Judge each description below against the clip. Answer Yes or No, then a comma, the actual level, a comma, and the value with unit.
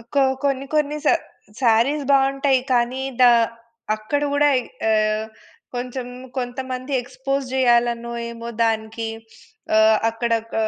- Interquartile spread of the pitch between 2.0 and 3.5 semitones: Yes, average, 2.9 semitones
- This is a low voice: No, high, 245 Hz